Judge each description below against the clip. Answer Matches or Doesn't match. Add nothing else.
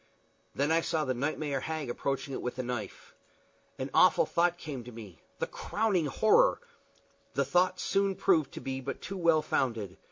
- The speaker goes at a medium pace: Matches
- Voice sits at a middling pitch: Matches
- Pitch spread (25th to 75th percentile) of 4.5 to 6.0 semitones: Matches